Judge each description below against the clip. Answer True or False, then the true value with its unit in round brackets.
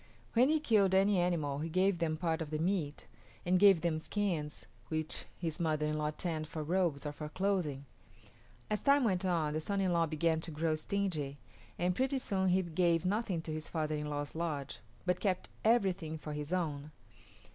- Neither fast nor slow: True (195 wpm)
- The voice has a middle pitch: True (165 Hz)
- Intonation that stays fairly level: False (3.6 semitones)